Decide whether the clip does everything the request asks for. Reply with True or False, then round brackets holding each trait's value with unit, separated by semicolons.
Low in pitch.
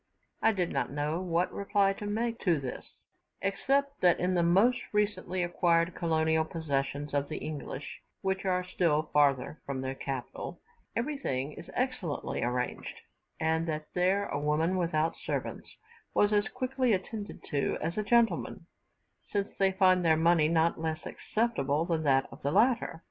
False (170 Hz)